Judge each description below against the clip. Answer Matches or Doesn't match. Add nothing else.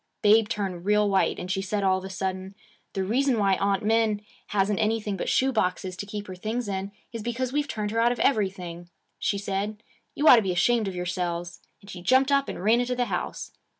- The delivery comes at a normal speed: Doesn't match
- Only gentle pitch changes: Doesn't match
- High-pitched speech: Matches